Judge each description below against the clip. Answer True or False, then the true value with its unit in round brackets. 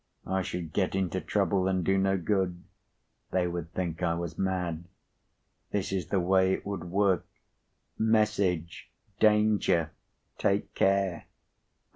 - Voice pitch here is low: True (95 Hz)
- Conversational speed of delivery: False (125 wpm)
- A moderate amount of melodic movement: False (2.1 semitones)